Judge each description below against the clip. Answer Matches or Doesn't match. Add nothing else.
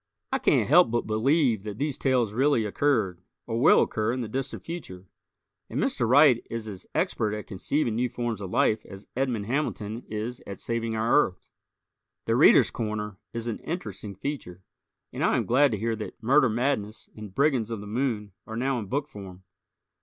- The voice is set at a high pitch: Doesn't match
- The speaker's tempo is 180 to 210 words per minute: Matches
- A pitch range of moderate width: Matches